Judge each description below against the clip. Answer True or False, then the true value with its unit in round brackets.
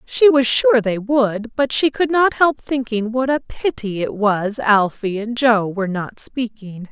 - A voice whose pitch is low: False (235 Hz)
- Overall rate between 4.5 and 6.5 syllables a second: False (4.0 syllables/s)